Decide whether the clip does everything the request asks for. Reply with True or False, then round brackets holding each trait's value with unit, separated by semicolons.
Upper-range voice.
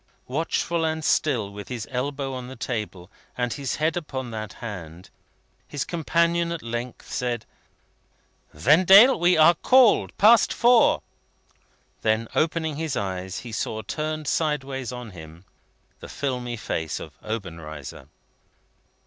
False (130 Hz)